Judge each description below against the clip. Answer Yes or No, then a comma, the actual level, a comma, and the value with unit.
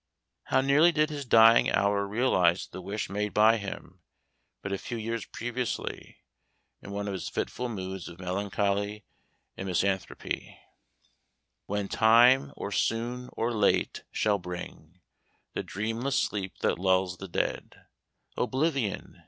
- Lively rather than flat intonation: No, average, 3.7 semitones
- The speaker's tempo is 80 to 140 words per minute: Yes, slow, 135 wpm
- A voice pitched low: Yes, low, 105 Hz